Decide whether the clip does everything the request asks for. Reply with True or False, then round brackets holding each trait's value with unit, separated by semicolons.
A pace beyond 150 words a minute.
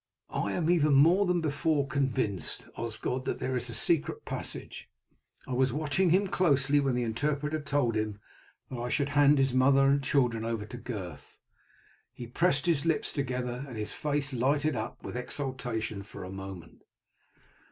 True (170 wpm)